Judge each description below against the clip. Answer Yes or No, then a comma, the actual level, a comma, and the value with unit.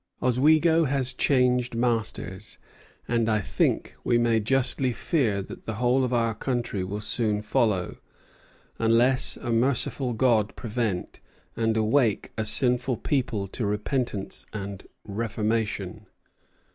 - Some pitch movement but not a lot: Yes, average, 3.0 semitones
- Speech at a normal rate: No, slow, 120 wpm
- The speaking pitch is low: Yes, low, 115 Hz